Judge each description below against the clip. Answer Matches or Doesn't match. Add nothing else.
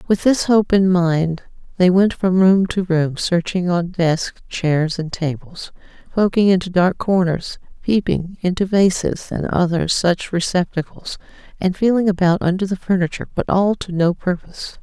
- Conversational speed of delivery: Matches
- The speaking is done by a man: Doesn't match